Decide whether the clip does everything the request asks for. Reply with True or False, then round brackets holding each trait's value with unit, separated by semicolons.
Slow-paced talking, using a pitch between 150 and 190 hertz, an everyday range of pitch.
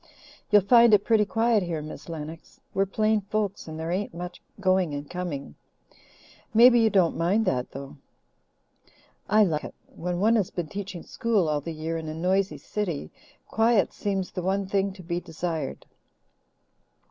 False (170 wpm; 185 Hz; 4.2 semitones)